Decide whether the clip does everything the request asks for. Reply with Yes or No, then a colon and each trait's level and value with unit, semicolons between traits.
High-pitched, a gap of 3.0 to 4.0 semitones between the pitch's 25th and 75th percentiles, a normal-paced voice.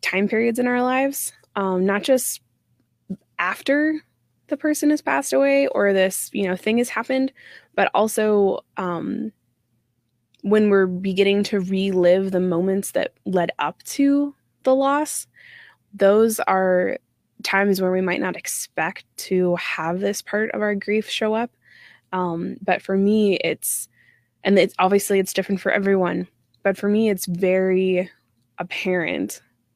Yes: high, 195 Hz; average, 3.5 semitones; average, 145 wpm